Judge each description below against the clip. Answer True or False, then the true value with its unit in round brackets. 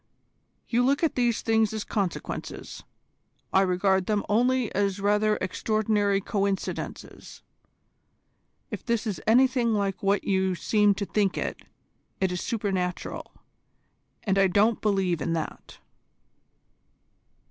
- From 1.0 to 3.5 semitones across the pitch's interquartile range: True (2.5 semitones)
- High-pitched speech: True (205 Hz)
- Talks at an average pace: False (120 wpm)